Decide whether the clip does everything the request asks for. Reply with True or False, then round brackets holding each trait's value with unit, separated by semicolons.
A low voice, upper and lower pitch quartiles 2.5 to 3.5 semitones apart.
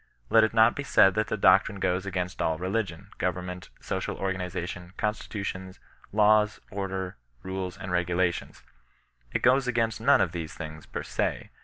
True (95 Hz; 2.9 semitones)